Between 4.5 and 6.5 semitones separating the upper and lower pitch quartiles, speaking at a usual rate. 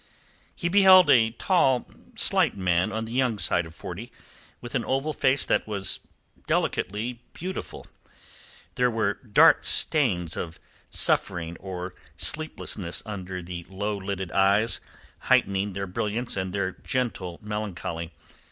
No: average, 4.8 semitones; slow, 130 wpm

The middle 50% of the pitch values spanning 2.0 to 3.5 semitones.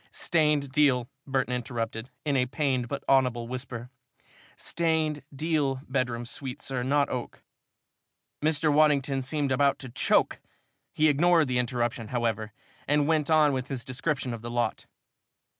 Yes: average, 3.2 semitones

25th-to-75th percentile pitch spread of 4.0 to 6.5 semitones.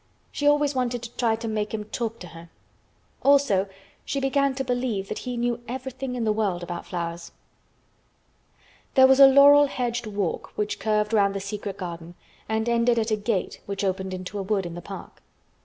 Yes: average, 4.3 semitones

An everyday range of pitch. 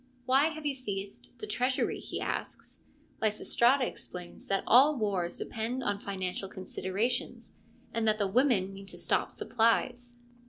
Yes: average, 4.5 semitones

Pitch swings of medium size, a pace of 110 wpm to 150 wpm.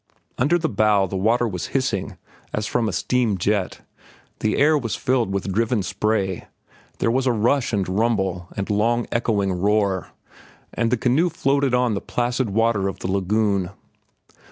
No: average, 3.9 semitones; average, 165 wpm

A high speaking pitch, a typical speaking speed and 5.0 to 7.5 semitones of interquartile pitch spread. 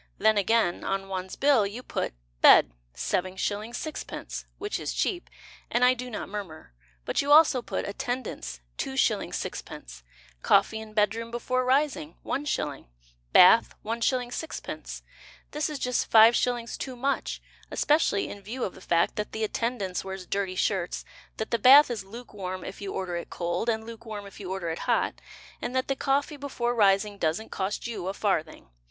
No: high, 220 Hz; average, 165 wpm; average, 4.6 semitones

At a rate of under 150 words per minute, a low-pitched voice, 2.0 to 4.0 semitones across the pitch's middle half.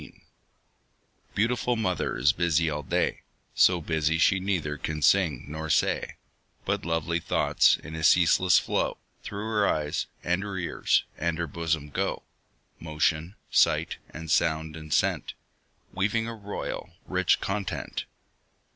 Yes: average, 140 wpm; very low, 85 Hz; average, 3.6 semitones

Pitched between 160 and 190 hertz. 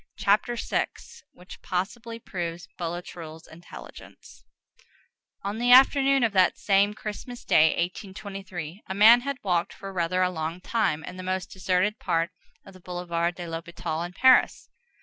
Yes: medium, 185 Hz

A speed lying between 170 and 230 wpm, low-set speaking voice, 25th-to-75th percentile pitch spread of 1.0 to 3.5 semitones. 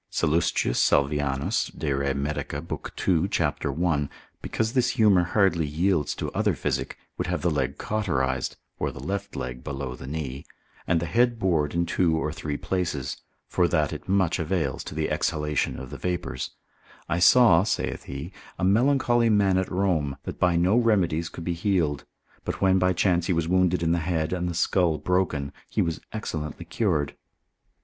No: average, 180 wpm; very low, 85 Hz; average, 4.1 semitones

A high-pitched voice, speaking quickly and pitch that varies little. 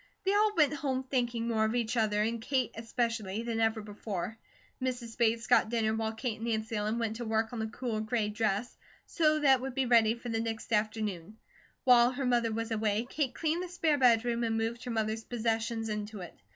Yes: high, 230 Hz; fast, 215 wpm; narrow, 2.0 semitones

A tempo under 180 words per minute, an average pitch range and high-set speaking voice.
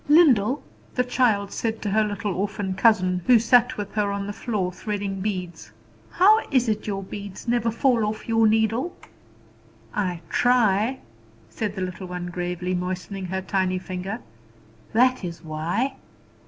Yes: average, 155 wpm; average, 3.8 semitones; high, 205 Hz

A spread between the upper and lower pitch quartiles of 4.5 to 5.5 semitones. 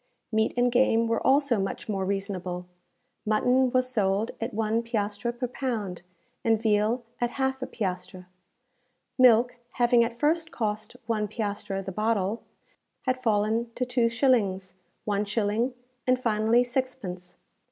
No: average, 3.2 semitones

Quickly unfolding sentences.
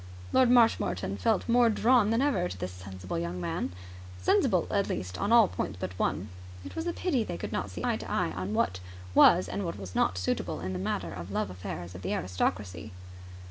Yes: fast, 220 wpm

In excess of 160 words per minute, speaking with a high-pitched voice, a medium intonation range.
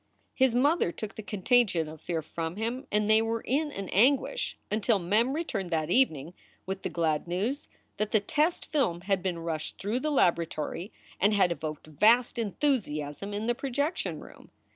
No: average, 180 wpm; high, 205 Hz; wide, 6.5 semitones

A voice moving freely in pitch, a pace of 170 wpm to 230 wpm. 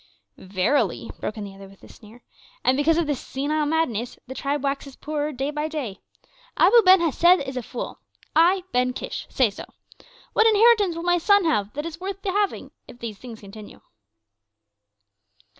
Yes: wide, 6.4 semitones; average, 185 wpm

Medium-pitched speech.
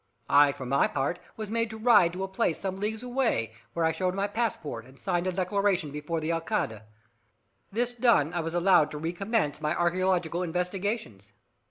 Yes: medium, 180 Hz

